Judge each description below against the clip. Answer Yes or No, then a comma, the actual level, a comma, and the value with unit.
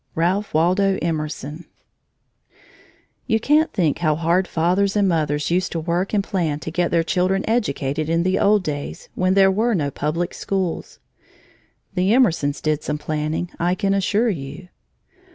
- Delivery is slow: No, average, 155 wpm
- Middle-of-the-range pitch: Yes, medium, 175 Hz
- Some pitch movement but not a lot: Yes, average, 3.9 semitones